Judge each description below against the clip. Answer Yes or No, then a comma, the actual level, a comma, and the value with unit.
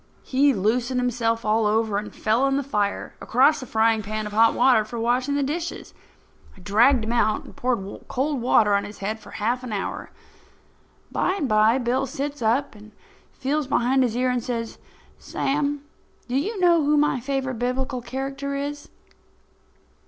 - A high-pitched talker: Yes, very high, 250 Hz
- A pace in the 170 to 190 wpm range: Yes, average, 175 wpm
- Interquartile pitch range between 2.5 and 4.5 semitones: Yes, average, 3.8 semitones